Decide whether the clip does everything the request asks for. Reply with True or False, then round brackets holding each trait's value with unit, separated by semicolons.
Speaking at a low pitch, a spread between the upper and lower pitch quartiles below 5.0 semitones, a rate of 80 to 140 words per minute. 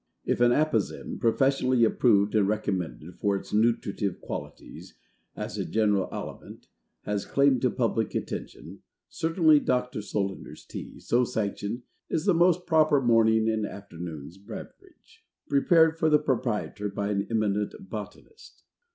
False (110 Hz; 5.4 semitones; 135 wpm)